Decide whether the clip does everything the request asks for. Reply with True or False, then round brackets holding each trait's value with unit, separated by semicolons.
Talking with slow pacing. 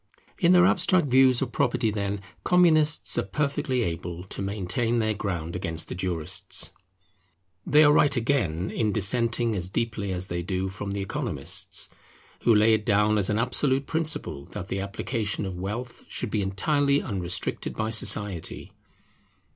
False (155 wpm)